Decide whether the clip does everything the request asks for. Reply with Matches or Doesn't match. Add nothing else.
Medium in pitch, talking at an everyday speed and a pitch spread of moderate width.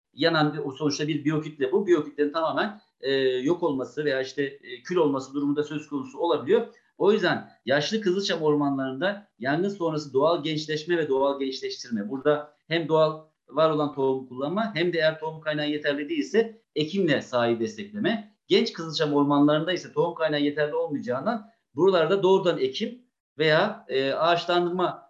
Doesn't match